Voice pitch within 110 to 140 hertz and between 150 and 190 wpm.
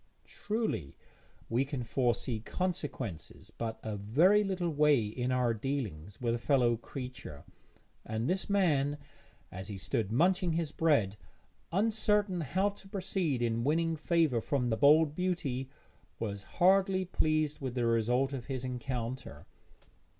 No: low, 135 Hz; slow, 135 wpm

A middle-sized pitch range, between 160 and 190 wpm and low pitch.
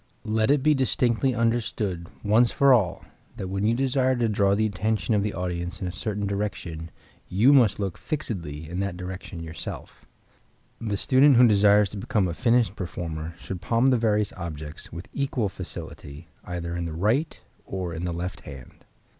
Yes: average, 4.9 semitones; average, 180 wpm; low, 100 Hz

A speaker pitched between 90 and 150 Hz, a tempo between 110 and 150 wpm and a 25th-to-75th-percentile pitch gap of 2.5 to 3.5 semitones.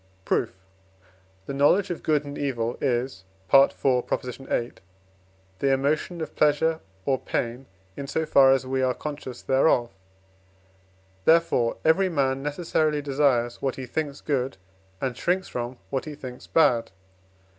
Yes: low, 135 Hz; slow, 135 wpm; average, 3.0 semitones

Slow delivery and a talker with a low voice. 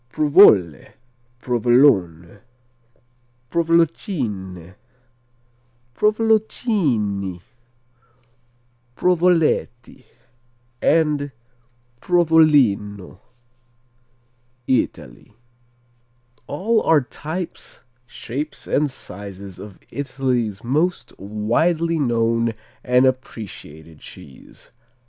Yes: slow, 55 wpm; low, 130 Hz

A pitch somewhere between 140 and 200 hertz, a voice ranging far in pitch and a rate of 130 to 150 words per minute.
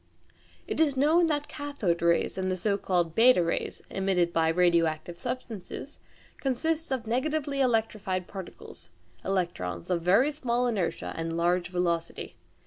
Yes: high, 190 Hz; wide, 7.0 semitones; slow, 135 wpm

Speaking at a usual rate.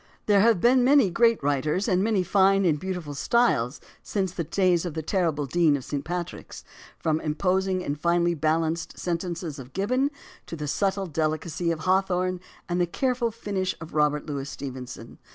Yes: average, 180 wpm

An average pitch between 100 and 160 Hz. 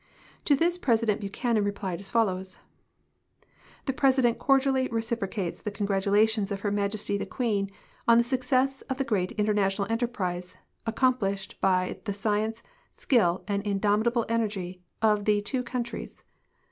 No: high, 215 Hz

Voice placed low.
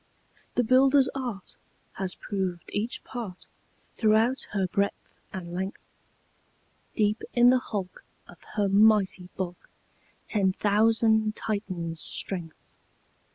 No: high, 205 Hz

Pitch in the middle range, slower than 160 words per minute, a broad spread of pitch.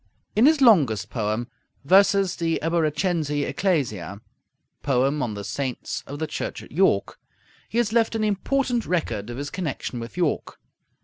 Yes: medium, 155 Hz; average, 150 wpm; wide, 8.0 semitones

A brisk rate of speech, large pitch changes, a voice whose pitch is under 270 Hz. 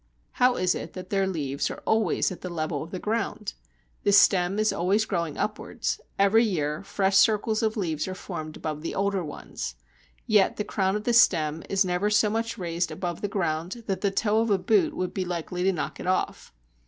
No: fast, 215 wpm; average, 3.6 semitones; high, 190 Hz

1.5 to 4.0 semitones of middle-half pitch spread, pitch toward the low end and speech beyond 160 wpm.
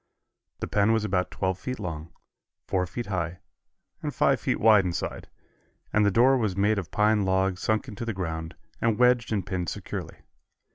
Yes: average, 3.2 semitones; low, 100 Hz; average, 180 wpm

